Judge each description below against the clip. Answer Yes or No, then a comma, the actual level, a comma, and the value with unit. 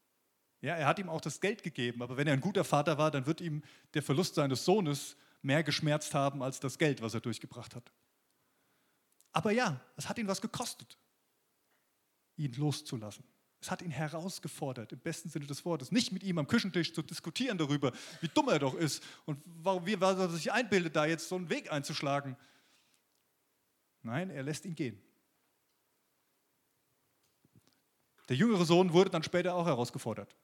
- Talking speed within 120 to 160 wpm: No, average, 175 wpm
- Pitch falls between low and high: Yes, medium, 160 Hz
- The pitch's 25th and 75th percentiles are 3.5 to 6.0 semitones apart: Yes, average, 4.3 semitones